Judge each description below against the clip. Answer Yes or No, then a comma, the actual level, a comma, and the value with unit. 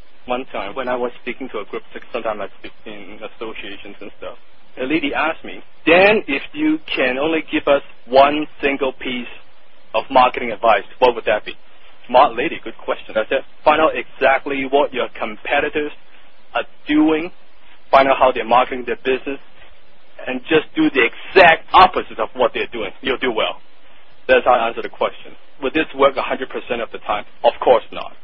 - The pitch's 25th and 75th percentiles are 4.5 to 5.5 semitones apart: No, average, 3.4 semitones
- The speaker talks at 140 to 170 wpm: No, average, 185 wpm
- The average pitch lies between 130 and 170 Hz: Yes, medium, 140 Hz